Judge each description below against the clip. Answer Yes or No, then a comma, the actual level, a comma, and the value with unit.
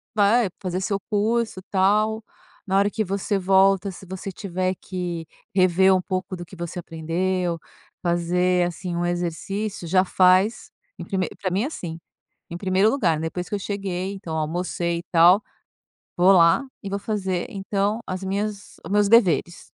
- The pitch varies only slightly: Yes, narrow, 2.2 semitones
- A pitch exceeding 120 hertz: Yes, medium, 185 Hz